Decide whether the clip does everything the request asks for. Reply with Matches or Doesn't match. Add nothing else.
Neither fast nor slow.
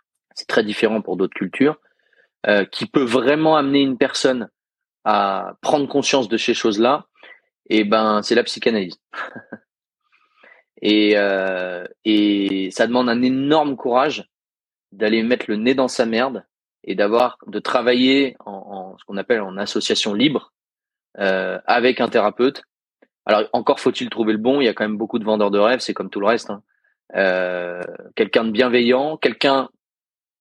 Matches